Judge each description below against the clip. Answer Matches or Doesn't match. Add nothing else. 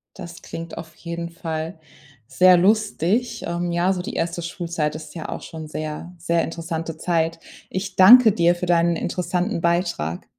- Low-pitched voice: Doesn't match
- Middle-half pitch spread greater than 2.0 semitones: Doesn't match